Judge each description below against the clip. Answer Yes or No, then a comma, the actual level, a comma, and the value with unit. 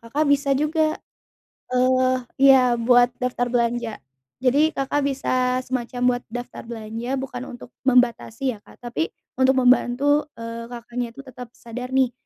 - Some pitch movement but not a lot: No, narrow, 1.9 semitones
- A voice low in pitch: No, very high, 250 Hz